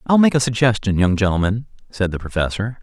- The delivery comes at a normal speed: Yes, average, 190 wpm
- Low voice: Yes, low, 110 Hz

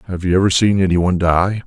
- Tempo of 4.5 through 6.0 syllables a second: No, 6.8 syllables/s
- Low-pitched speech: Yes, very low, 90 Hz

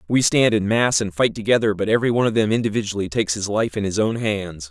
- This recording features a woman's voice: No, male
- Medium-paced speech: No, fast, 255 wpm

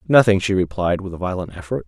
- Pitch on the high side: No, very low, 95 Hz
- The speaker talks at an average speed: No, fast, 225 wpm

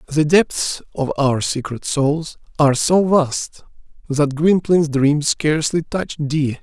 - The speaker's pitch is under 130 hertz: No, medium, 150 Hz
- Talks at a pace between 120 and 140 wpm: Yes, slow, 135 wpm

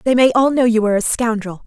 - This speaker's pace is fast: Yes, fast, 290 wpm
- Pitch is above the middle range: Yes, high, 230 Hz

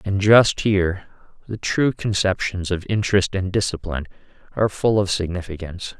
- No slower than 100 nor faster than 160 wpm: Yes, average, 140 wpm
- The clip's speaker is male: Yes, male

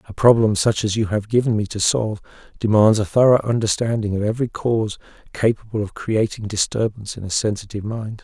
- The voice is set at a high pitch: No, low, 110 Hz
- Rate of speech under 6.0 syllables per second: No, 6.1 syllables/s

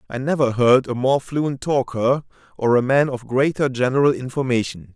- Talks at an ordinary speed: Yes, average, 170 wpm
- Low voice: Yes, low, 130 Hz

